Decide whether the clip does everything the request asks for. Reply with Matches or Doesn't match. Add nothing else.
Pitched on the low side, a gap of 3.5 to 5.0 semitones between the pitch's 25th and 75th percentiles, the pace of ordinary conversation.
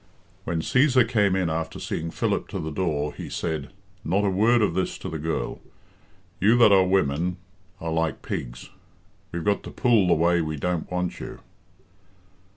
Matches